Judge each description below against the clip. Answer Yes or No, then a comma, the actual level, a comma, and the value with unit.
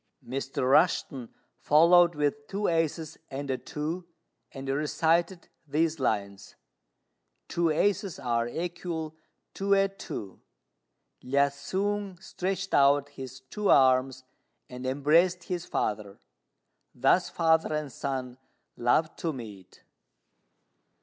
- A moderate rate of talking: No, slow, 110 wpm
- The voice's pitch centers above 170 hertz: No, medium, 150 Hz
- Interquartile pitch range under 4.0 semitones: No, average, 4.7 semitones